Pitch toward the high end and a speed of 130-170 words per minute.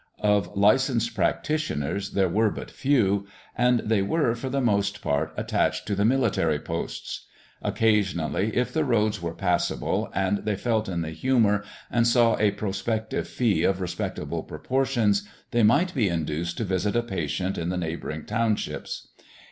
No: low, 105 Hz; average, 155 wpm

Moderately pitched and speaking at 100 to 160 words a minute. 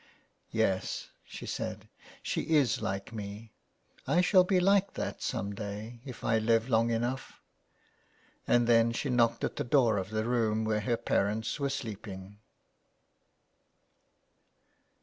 No: low, 115 Hz; average, 145 wpm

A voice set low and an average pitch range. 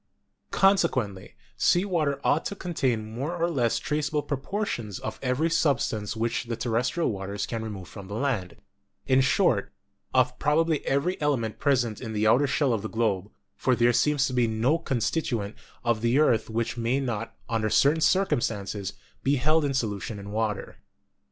Yes: low, 120 Hz; average, 4.9 semitones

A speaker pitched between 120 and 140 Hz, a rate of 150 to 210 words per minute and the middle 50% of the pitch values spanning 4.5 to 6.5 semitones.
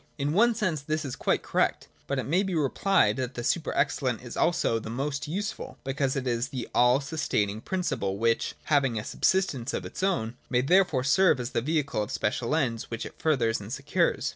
Yes: low, 135 Hz; fast, 205 wpm; average, 5.2 semitones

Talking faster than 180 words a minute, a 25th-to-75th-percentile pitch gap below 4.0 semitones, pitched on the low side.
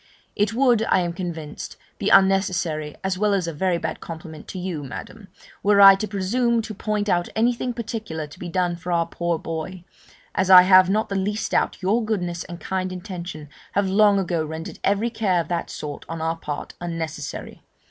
No: average, 195 wpm; average, 3.5 semitones; medium, 185 Hz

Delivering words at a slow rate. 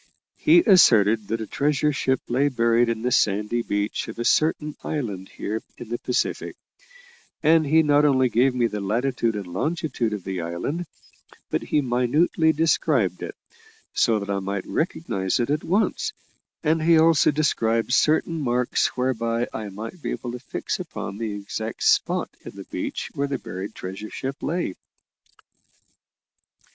No: average, 160 wpm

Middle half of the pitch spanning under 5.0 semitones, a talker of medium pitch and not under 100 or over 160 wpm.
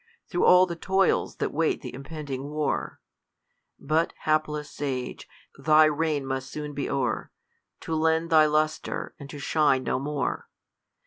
Yes: narrow, 2.4 semitones; medium, 150 Hz; average, 150 wpm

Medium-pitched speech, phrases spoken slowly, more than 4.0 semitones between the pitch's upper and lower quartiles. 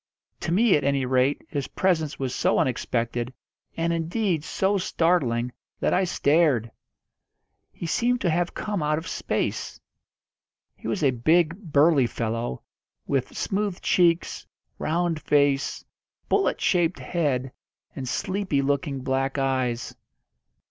Yes: medium, 150 Hz; slow, 130 wpm; average, 4.8 semitones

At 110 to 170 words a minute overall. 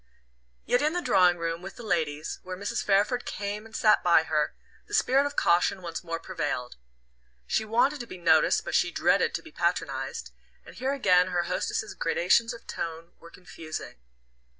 No: average, 180 wpm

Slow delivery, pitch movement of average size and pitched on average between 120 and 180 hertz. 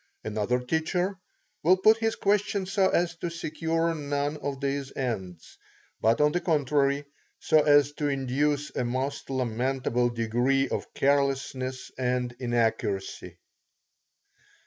Yes: slow, 125 wpm; average, 4.1 semitones; medium, 140 Hz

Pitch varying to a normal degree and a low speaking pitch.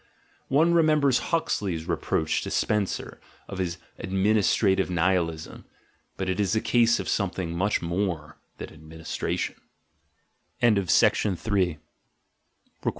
Yes: average, 4.3 semitones; very low, 95 Hz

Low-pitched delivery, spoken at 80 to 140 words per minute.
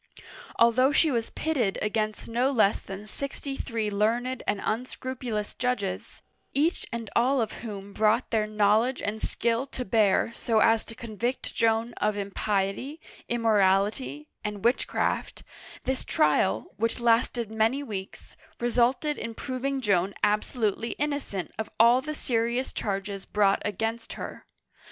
No: high, 225 Hz; slow, 135 wpm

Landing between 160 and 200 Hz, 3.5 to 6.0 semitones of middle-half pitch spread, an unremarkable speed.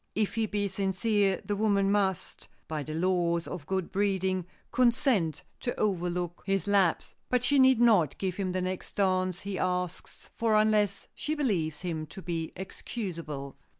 No: high, 190 Hz; average, 2.9 semitones; average, 160 wpm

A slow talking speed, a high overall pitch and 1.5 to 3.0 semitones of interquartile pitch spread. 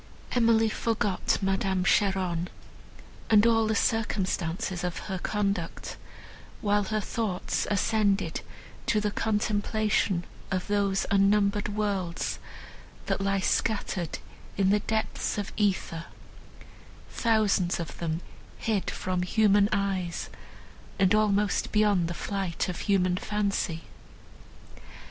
Yes: slow, 110 wpm; high, 200 Hz; narrow, 2.4 semitones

